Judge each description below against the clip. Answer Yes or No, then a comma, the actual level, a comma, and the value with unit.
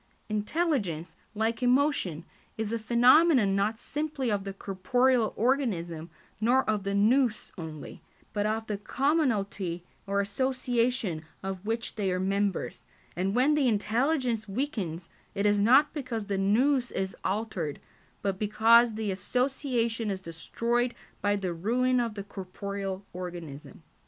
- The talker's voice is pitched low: No, high, 215 Hz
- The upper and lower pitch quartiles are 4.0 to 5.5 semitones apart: Yes, average, 4.3 semitones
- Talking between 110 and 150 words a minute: Yes, average, 140 wpm